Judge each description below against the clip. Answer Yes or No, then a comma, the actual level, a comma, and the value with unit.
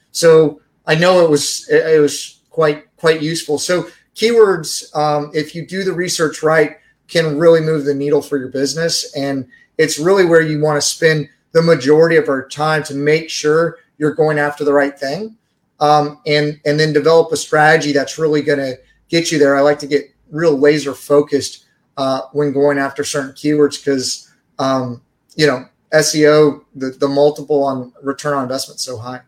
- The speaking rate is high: No, average, 185 wpm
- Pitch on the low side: No, medium, 150 Hz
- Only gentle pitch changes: Yes, narrow, 2.1 semitones